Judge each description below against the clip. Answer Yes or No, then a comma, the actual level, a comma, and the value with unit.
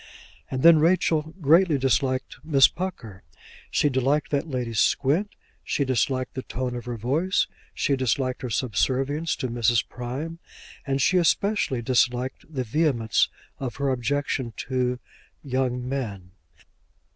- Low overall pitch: Yes, low, 130 Hz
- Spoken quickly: No, slow, 135 wpm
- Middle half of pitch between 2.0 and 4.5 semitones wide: Yes, average, 3.3 semitones